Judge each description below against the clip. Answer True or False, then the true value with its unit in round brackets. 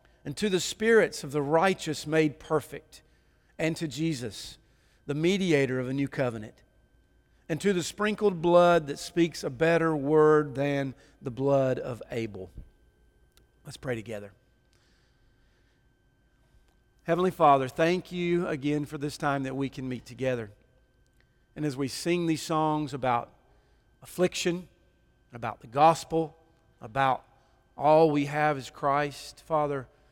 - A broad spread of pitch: False (4.0 semitones)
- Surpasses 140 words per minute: False (135 wpm)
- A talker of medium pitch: True (145 Hz)